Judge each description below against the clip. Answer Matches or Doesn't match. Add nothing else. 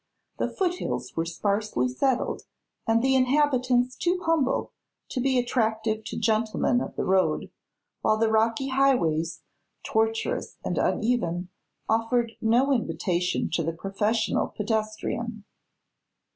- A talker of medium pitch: Doesn't match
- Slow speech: Matches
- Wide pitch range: Doesn't match